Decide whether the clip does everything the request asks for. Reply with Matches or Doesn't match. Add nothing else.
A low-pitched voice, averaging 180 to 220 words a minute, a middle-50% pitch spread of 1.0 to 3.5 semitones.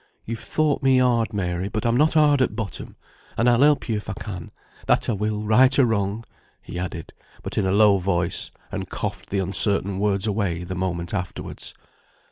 Doesn't match